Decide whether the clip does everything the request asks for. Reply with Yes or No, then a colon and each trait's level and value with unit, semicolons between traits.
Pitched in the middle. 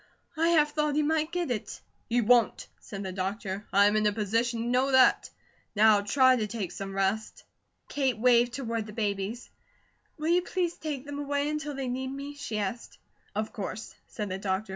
No: high, 235 Hz